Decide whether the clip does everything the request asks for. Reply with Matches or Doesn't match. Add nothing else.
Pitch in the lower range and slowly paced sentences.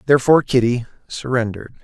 Matches